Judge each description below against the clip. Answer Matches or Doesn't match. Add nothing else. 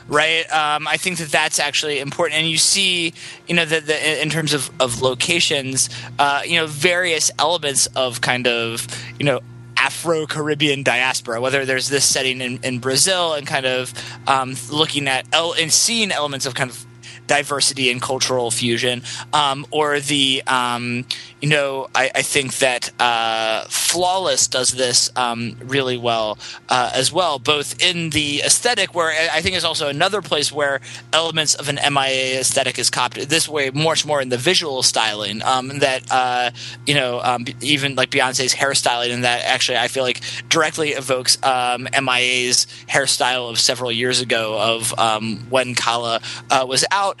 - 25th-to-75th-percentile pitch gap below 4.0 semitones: Matches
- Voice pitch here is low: Matches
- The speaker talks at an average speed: Matches